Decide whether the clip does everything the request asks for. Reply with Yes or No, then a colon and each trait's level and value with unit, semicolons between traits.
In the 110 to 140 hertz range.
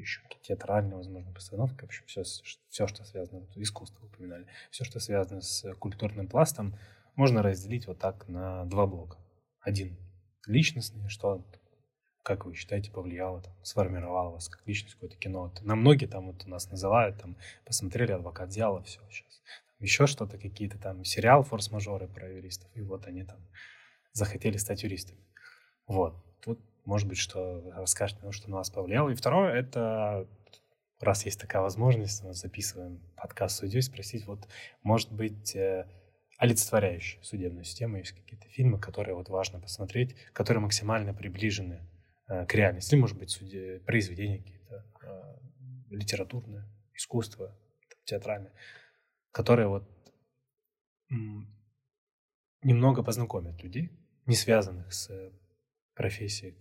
No: low, 100 Hz